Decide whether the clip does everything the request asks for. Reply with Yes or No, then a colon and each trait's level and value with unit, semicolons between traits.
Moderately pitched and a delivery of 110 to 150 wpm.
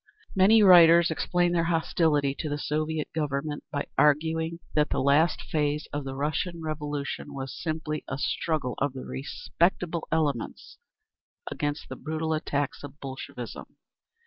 Yes: medium, 155 Hz; average, 140 wpm